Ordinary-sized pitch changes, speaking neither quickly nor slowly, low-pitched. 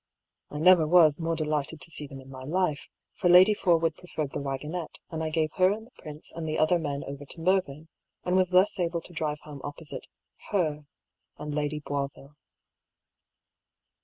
No: average, 3.2 semitones; average, 185 wpm; medium, 155 Hz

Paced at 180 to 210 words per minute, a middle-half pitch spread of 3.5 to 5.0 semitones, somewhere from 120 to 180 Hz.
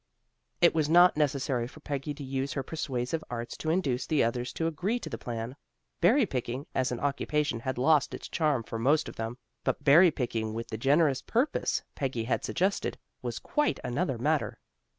Yes: average, 190 wpm; average, 4.4 semitones; medium, 140 Hz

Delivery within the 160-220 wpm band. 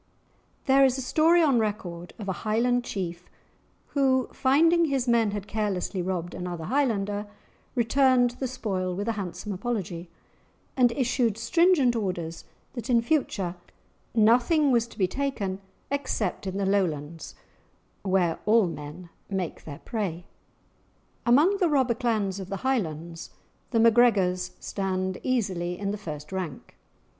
No: average, 140 wpm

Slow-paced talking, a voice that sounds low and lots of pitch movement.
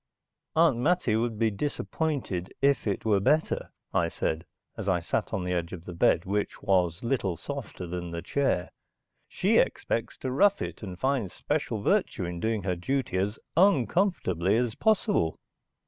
No: average, 165 wpm; low, 105 Hz; wide, 7.4 semitones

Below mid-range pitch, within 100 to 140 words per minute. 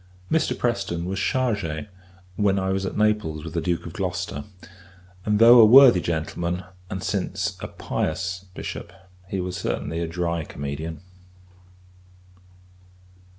Yes: very low, 90 Hz; slow, 135 wpm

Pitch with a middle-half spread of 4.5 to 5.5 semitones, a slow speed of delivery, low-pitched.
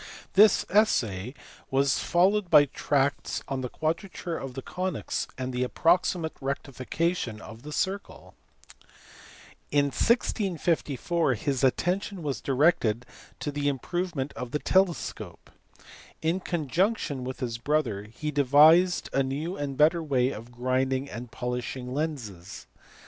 No: average, 5.0 semitones; slow, 125 wpm; medium, 145 Hz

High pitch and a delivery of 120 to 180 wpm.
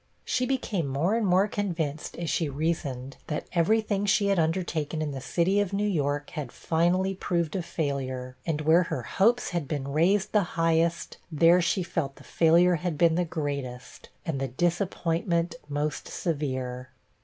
No: medium, 165 Hz; average, 170 wpm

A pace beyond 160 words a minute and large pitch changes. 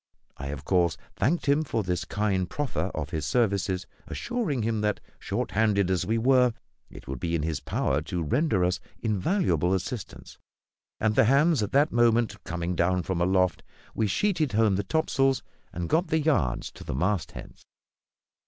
Yes: average, 170 wpm; wide, 6.7 semitones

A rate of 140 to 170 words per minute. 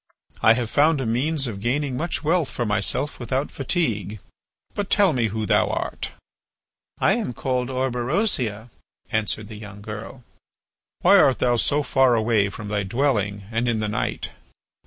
Yes: average, 160 wpm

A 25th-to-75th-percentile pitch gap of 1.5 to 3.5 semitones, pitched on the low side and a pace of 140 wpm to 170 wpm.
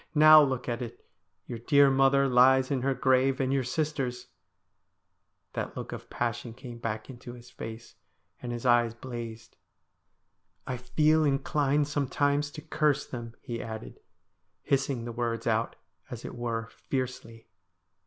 Yes: average, 2.7 semitones; low, 125 Hz; average, 155 wpm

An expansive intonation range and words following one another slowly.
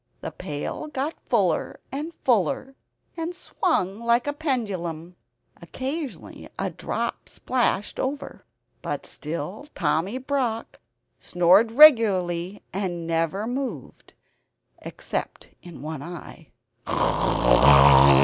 Yes: wide, 7.4 semitones; slow, 95 wpm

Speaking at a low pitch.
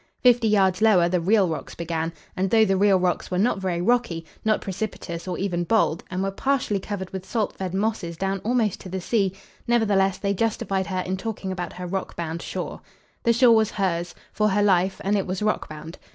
No: high, 195 Hz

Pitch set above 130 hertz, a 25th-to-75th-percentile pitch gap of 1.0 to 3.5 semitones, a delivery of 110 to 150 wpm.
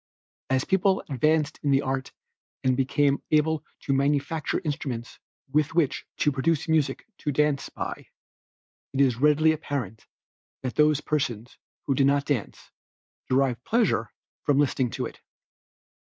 Yes: medium, 140 Hz; narrow, 2.4 semitones; slow, 135 wpm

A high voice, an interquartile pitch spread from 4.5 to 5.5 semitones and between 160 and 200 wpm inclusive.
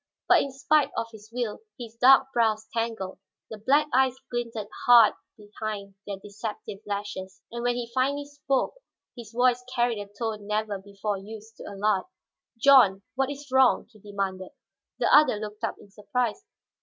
No: high, 225 Hz; average, 3.4 semitones; average, 165 wpm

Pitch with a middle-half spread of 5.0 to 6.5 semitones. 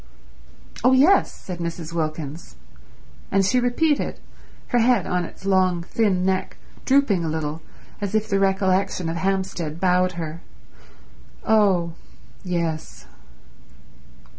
No: average, 3.2 semitones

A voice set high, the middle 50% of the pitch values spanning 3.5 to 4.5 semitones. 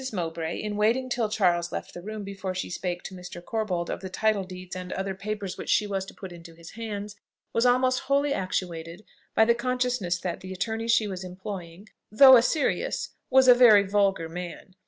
Yes: high, 195 Hz; average, 3.8 semitones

